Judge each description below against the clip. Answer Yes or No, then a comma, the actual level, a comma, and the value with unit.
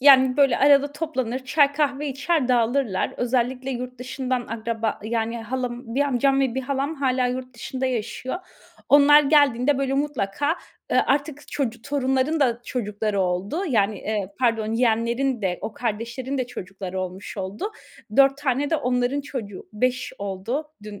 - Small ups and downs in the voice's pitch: No, average, 3.5 semitones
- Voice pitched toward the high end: Yes, very high, 255 Hz